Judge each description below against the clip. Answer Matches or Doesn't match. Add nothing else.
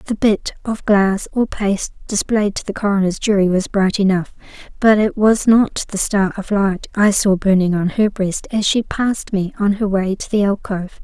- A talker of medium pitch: Doesn't match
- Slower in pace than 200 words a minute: Doesn't match